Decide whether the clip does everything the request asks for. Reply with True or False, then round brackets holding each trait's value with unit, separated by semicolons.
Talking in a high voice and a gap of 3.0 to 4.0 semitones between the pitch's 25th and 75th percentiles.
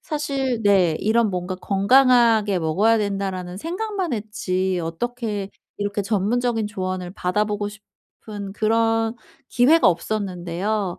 True (210 Hz; 3.4 semitones)